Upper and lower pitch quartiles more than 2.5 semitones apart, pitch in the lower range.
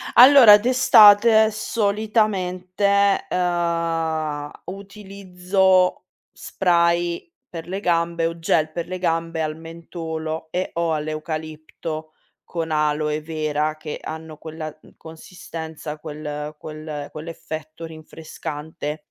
No: average, 2.9 semitones; medium, 165 Hz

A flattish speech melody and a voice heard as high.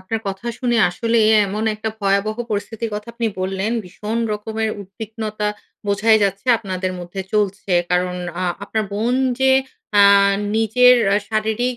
Yes: narrow, 2.3 semitones; high, 215 Hz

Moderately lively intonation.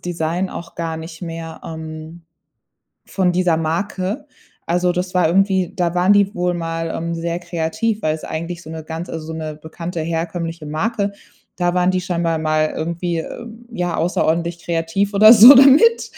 No: narrow, 2.2 semitones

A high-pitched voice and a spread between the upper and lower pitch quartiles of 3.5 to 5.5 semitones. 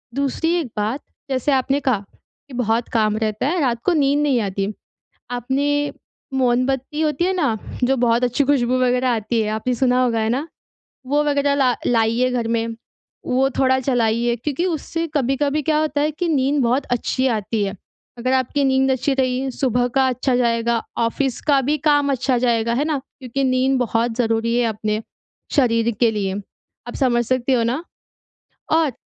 No: very high, 255 Hz; average, 3.1 semitones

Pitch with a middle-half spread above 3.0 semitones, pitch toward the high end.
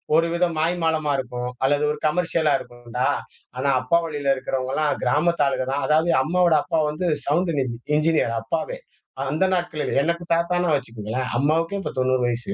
No: average, 4.5 semitones; medium, 150 Hz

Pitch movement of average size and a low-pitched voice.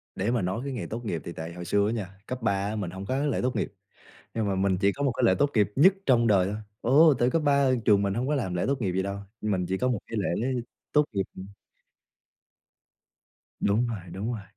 Yes: average, 4.8 semitones; low, 105 Hz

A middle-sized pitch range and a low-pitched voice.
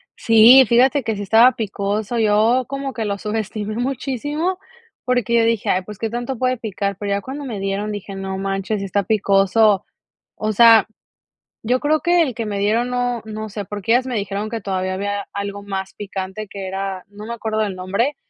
No: average, 3.2 semitones; high, 215 Hz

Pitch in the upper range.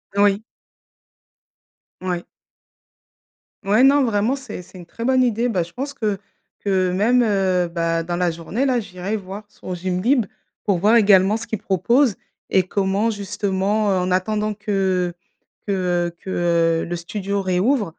Yes: high, 200 Hz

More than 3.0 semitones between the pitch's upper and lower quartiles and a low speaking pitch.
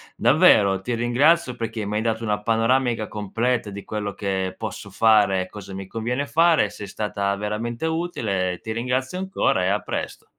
Yes: average, 3.4 semitones; low, 110 Hz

